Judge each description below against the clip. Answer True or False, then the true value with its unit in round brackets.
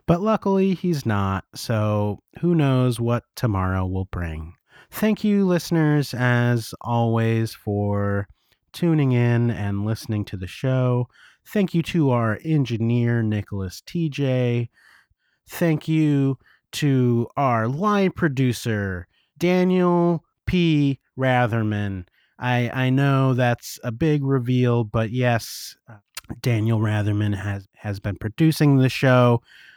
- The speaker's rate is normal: False (115 wpm)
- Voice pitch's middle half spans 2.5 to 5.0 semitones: False (5.5 semitones)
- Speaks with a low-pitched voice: True (120 Hz)